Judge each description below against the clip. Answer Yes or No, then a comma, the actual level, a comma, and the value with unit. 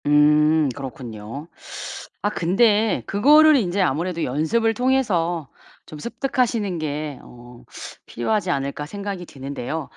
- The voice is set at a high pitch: No, medium, 165 Hz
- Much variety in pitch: Yes, wide, 6.5 semitones